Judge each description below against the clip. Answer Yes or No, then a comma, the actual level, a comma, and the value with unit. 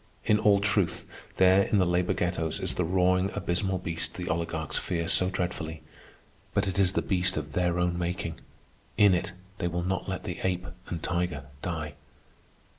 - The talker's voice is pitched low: Yes, very low, 90 Hz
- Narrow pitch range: Yes, narrow, 1.7 semitones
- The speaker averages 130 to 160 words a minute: No, average, 175 wpm